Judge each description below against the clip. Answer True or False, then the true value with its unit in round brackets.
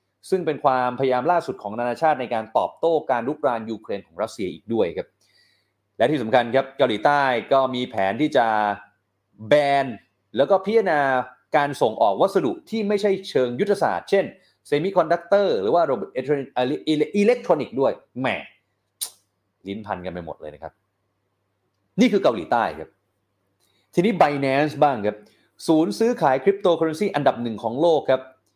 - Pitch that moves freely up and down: True (7.6 semitones)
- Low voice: True (130 Hz)